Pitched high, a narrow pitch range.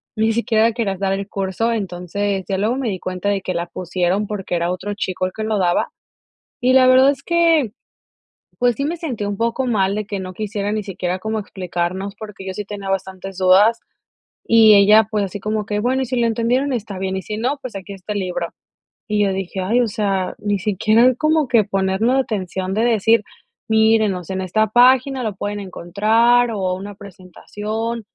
No: high, 205 Hz; average, 3.2 semitones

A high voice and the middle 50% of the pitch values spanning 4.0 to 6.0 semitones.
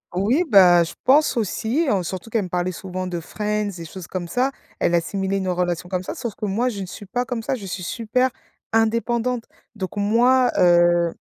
Yes: high, 200 Hz; average, 4.5 semitones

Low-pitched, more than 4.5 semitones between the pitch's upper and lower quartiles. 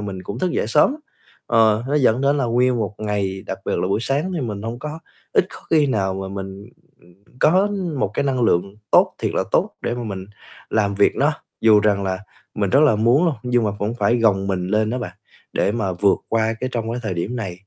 No: low, 110 Hz; average, 4.1 semitones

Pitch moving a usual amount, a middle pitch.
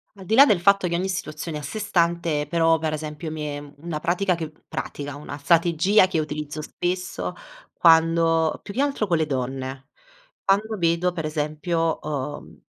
Yes: average, 3.1 semitones; medium, 165 Hz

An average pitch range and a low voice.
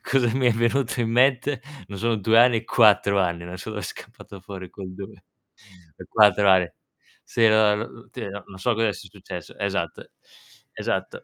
Yes: average, 3.1 semitones; low, 110 Hz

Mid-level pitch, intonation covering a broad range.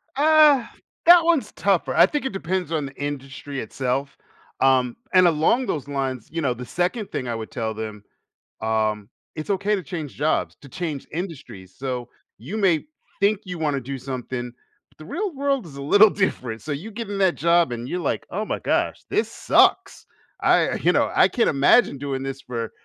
Yes: medium, 150 Hz; wide, 7.3 semitones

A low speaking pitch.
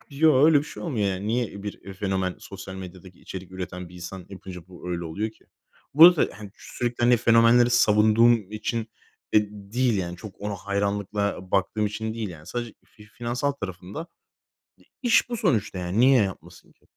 Yes: low, 105 Hz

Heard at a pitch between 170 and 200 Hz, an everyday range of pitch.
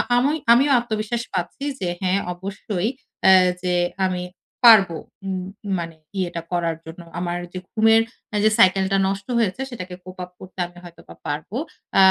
Yes: medium, 185 Hz; average, 3.4 semitones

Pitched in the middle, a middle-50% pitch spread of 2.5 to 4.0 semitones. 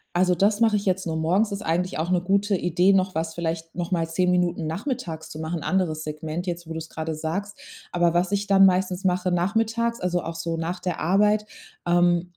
Yes: medium, 180 Hz; average, 2.8 semitones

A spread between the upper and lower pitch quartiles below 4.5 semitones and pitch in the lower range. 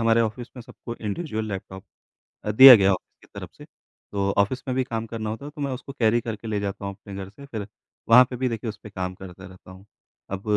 Yes: average, 3.8 semitones; low, 110 Hz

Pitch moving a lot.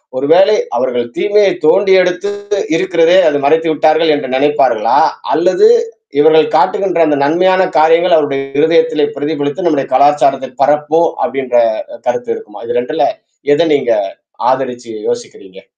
No: average, 4.2 semitones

